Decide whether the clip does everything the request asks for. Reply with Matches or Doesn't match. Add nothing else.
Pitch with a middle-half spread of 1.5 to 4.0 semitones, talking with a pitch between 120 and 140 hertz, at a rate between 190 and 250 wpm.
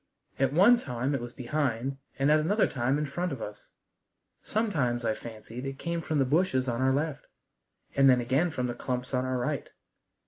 Matches